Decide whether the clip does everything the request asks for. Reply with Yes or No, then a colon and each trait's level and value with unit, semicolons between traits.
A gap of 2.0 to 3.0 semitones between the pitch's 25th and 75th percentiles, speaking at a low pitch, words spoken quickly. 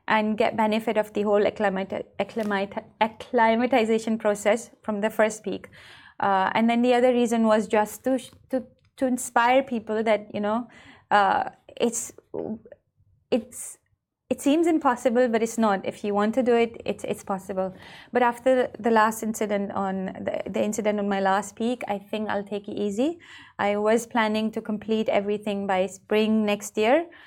No: narrow, 2.6 semitones; high, 220 Hz; fast, 165 wpm